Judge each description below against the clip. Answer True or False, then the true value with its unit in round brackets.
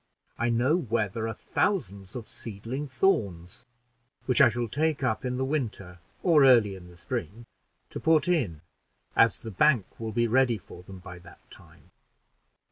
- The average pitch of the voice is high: False (115 Hz)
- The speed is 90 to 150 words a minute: False (170 wpm)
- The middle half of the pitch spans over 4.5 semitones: True (5.2 semitones)